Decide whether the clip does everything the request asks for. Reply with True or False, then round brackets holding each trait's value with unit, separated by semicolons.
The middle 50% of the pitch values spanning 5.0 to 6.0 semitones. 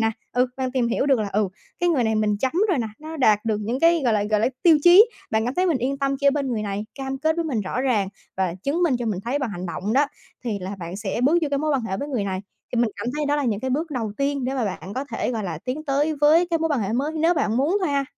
True (5.4 semitones)